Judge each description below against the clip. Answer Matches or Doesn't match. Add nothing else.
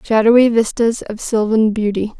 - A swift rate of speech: Doesn't match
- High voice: Matches